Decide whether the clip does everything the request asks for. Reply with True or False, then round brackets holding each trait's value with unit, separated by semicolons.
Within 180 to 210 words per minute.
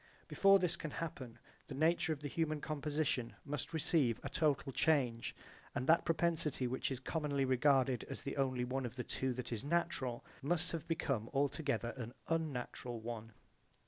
False (170 wpm)